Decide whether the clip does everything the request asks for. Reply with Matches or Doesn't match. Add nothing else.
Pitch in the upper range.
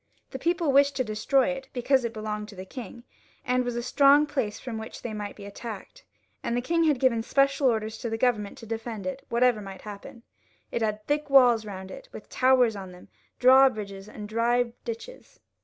Matches